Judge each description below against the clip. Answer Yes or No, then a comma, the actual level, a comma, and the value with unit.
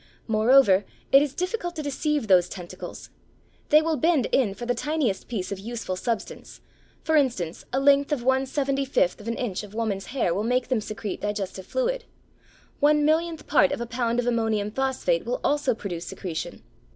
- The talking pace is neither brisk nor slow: Yes, average, 185 wpm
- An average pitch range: No, wide, 5.9 semitones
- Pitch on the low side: No, high, 245 Hz